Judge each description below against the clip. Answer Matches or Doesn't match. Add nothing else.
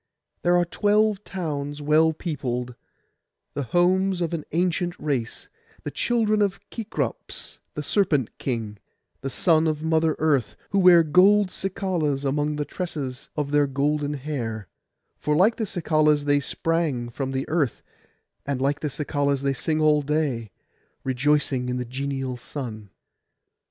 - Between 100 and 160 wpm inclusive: Matches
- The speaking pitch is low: Doesn't match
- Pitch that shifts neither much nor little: Matches